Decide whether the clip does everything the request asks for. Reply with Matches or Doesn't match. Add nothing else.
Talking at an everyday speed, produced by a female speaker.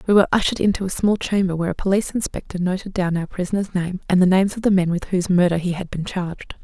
Doesn't match